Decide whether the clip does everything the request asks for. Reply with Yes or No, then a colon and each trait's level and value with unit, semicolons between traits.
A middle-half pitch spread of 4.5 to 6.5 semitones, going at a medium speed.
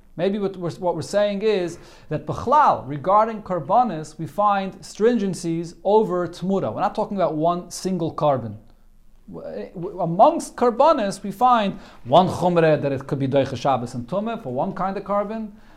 Yes: average, 4.9 semitones; average, 160 wpm